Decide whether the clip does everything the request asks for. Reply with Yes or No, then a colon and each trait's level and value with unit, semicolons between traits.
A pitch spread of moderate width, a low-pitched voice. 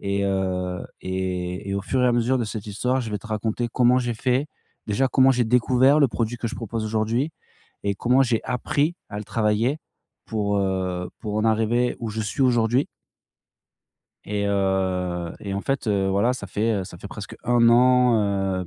Yes: average, 3.9 semitones; low, 110 Hz